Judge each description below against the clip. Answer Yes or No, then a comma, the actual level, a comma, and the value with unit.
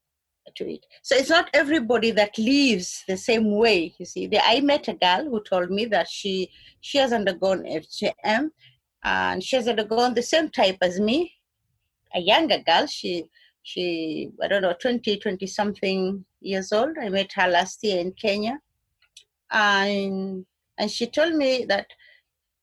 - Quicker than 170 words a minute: No, average, 160 wpm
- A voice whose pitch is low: No, high, 205 Hz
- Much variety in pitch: No, average, 4.3 semitones